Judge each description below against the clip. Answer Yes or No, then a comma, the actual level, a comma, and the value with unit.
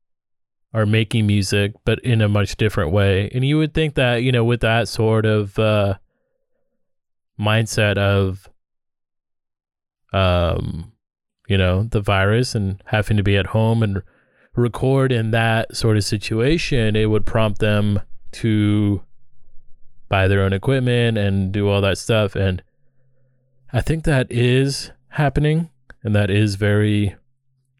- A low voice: Yes, low, 110 Hz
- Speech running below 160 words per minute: Yes, average, 140 wpm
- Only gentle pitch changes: No, average, 3.6 semitones